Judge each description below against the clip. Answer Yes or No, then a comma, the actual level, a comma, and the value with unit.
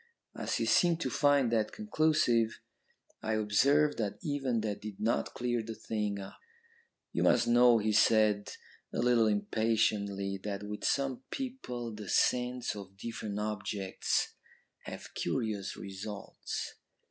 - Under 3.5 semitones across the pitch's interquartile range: Yes, average, 3.1 semitones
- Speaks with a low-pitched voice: Yes, low, 110 Hz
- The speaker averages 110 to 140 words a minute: Yes, slow, 135 wpm